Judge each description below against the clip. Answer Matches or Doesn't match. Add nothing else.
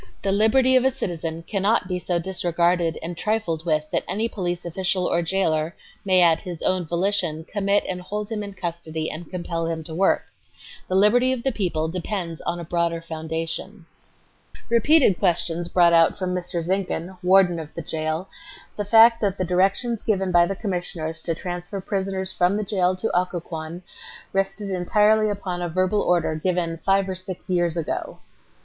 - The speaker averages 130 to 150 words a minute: Doesn't match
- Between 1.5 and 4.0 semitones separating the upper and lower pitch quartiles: Matches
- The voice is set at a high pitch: Doesn't match